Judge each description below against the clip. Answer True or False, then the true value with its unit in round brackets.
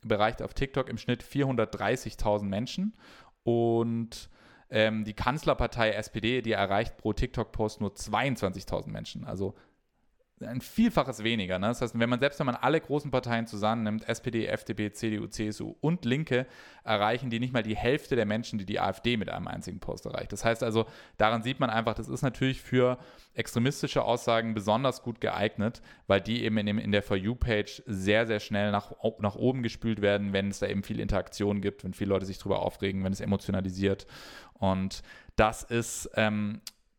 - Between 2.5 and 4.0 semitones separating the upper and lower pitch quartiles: True (2.8 semitones)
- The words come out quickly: False (180 wpm)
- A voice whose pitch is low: True (110 Hz)